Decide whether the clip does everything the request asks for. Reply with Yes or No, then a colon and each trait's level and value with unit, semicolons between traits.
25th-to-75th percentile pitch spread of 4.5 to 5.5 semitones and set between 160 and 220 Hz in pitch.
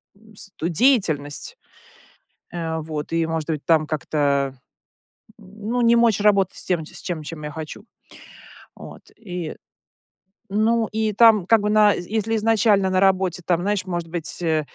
Yes: average, 4.9 semitones; medium, 185 Hz